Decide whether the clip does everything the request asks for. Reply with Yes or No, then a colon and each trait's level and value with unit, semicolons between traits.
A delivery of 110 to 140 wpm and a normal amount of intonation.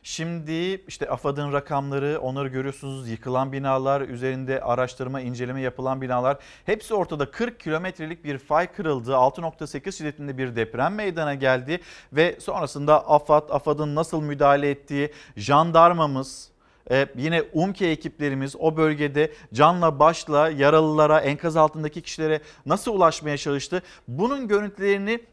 Yes: average, 120 wpm; average, 3.0 semitones